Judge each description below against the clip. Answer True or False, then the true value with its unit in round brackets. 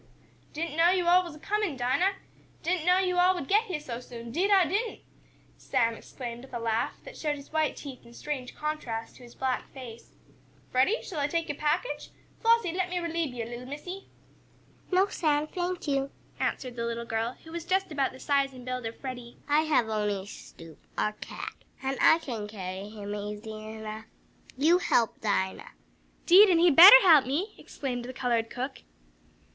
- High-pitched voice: True (275 Hz)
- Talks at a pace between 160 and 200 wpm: True (195 wpm)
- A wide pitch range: True (6.8 semitones)